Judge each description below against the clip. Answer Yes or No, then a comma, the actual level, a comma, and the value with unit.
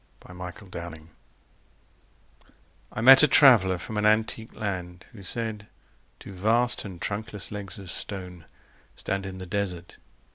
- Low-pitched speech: Yes, low, 100 Hz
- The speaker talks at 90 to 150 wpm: Yes, average, 140 wpm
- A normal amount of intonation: Yes, average, 3.3 semitones